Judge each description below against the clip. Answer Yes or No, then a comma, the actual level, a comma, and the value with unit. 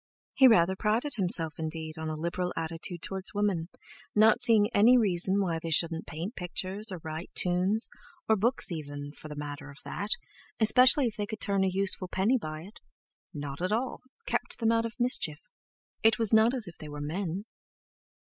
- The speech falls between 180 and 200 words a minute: Yes, average, 185 wpm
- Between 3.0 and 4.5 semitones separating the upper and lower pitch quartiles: No, average, 5.2 semitones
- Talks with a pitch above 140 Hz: Yes, high, 190 Hz